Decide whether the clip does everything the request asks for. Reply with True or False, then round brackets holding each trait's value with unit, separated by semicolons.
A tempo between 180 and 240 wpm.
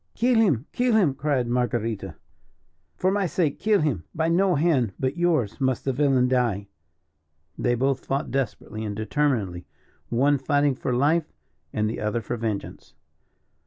False (155 wpm)